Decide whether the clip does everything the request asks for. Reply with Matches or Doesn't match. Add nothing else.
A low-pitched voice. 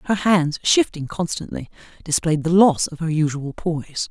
Doesn't match